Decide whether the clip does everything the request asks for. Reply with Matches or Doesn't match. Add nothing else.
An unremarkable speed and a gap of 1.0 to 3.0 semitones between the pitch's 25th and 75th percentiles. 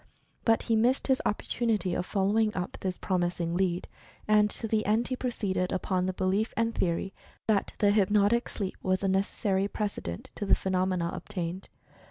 Matches